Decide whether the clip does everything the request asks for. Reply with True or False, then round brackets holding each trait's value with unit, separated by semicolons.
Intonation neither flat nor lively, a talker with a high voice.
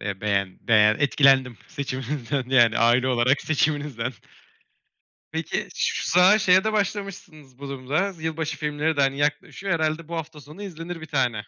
False (4.1 semitones; 145 Hz)